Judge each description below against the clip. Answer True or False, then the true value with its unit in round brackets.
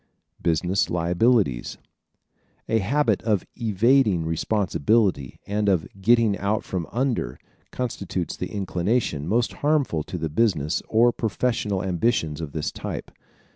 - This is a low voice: True (100 Hz)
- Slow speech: True (125 wpm)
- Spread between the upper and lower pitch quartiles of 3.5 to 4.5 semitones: False (5.5 semitones)